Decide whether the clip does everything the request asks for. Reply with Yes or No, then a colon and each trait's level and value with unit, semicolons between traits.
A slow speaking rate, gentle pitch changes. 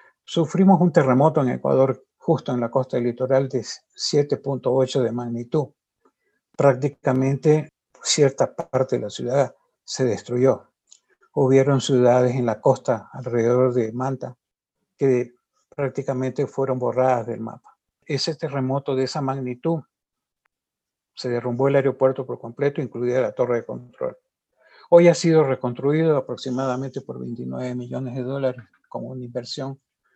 Yes: slow, 130 wpm; narrow, 2.1 semitones